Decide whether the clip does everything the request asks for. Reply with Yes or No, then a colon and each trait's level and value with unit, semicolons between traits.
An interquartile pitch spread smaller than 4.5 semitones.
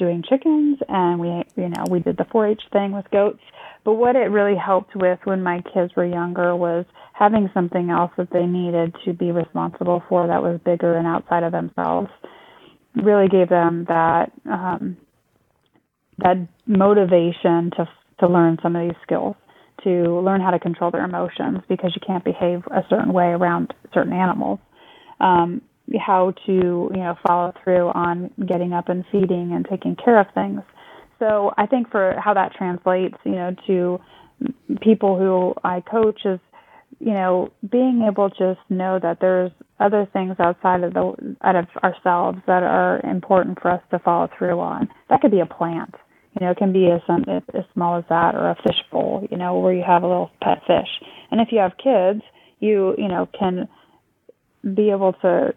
Yes: narrow, 2.5 semitones